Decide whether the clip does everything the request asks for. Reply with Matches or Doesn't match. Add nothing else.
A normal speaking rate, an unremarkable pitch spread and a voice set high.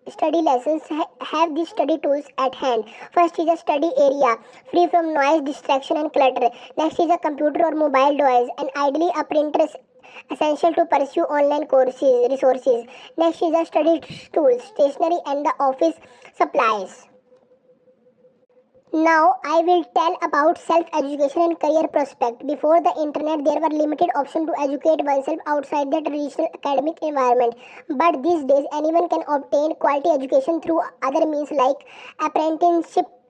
Matches